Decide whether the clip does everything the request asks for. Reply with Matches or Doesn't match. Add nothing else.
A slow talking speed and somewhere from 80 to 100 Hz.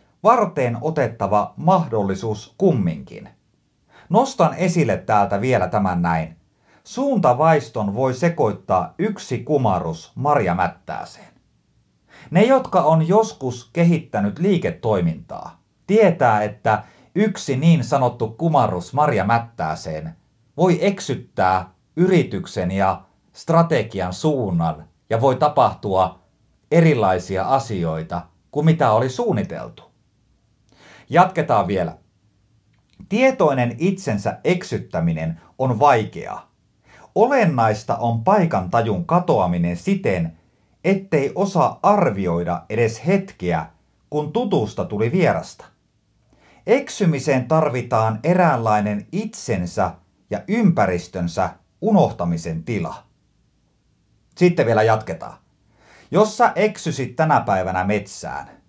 Doesn't match